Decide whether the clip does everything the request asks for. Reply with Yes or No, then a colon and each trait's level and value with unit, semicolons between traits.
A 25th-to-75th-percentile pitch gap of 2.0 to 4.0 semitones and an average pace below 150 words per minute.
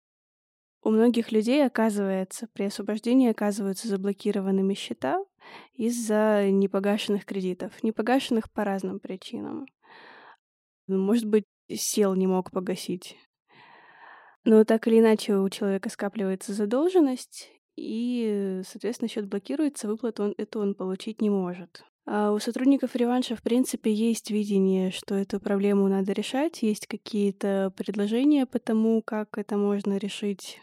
Yes: average, 2.9 semitones; average, 125 wpm